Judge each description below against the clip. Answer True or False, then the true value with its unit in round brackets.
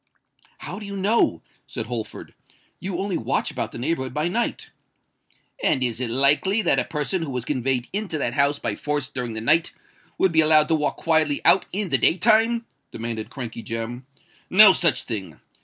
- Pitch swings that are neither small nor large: False (7.0 semitones)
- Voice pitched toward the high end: False (150 Hz)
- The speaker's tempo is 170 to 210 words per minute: True (190 wpm)